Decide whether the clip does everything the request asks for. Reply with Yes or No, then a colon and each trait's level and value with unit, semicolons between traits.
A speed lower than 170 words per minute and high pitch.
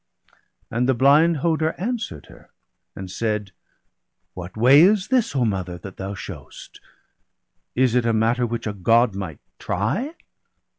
No: average, 155 wpm; low, 115 Hz